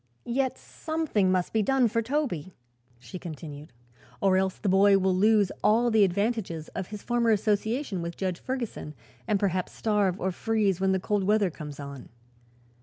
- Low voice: No, high, 200 Hz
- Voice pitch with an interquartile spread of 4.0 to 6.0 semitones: No, average, 3.4 semitones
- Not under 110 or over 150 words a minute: No, average, 170 wpm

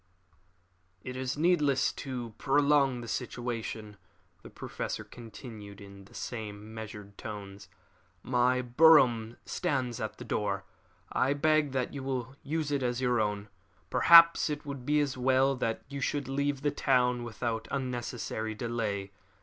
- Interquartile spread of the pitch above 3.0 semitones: Yes, average, 3.9 semitones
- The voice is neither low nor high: No, low, 125 Hz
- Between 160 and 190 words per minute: No, average, 140 wpm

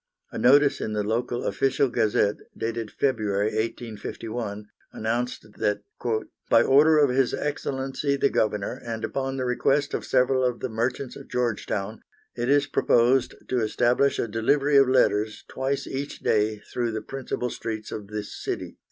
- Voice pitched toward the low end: Yes, low, 120 Hz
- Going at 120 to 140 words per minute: No, average, 155 wpm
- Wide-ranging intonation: No, average, 3.5 semitones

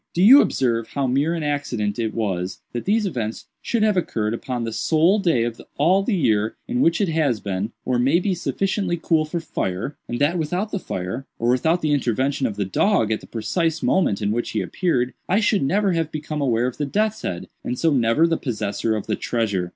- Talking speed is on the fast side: Yes, fast, 220 wpm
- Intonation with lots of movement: Yes, wide, 7.1 semitones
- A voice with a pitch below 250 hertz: Yes, medium, 140 Hz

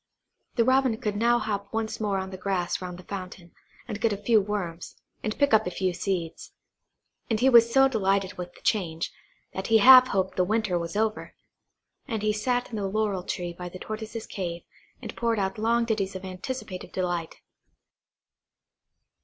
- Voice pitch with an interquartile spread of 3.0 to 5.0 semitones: Yes, average, 3.4 semitones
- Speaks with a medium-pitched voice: No, high, 205 Hz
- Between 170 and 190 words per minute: Yes, average, 185 wpm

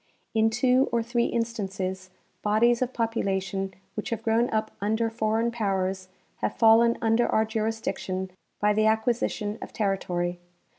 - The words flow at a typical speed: Yes, average, 145 wpm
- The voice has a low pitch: No, high, 220 Hz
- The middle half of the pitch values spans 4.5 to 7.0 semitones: No, average, 2.9 semitones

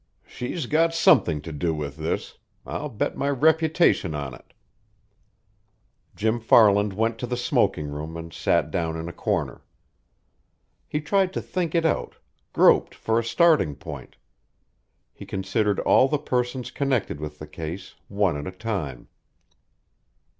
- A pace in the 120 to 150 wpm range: Yes, average, 145 wpm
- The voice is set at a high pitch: No, low, 105 Hz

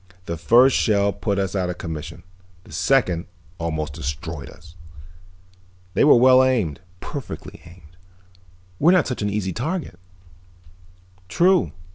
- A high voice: No, very low, 95 Hz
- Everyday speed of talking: No, slow, 130 wpm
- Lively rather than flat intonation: Yes, wide, 7.6 semitones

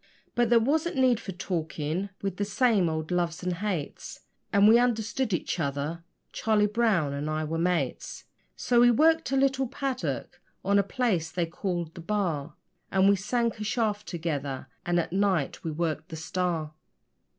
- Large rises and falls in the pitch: Yes, wide, 5.7 semitones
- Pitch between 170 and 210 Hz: Yes, high, 190 Hz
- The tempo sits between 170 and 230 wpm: Yes, average, 175 wpm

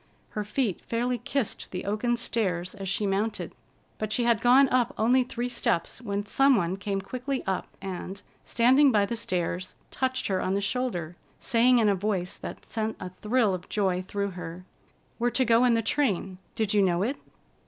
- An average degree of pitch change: Yes, average, 4.2 semitones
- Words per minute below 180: No, average, 190 wpm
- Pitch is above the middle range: Yes, high, 210 Hz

